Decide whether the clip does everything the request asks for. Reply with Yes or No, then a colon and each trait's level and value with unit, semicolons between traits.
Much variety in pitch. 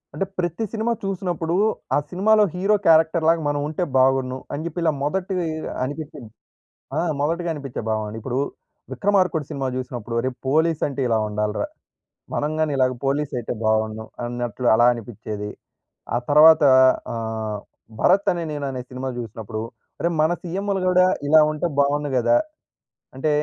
Yes: wide, 5.7 semitones